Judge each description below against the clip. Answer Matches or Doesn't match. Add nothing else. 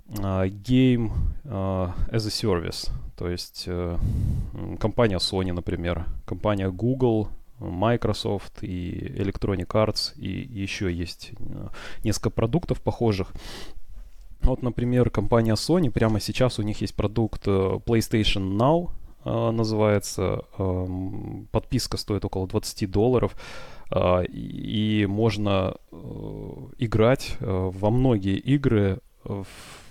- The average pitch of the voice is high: Doesn't match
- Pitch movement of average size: Matches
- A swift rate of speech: Doesn't match